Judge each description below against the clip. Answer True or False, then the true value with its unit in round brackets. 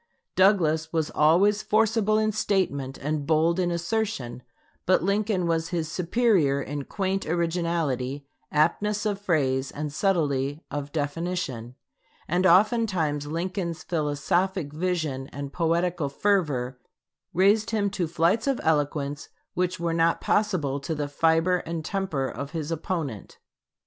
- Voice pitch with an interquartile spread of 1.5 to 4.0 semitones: False (4.5 semitones)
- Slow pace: True (130 wpm)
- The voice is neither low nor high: True (165 Hz)